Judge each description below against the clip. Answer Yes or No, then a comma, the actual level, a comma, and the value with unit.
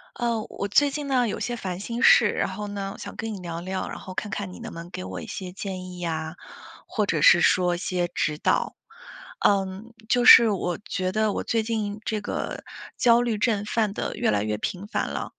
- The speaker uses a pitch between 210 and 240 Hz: No, high, 200 Hz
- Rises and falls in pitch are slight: No, average, 3.8 semitones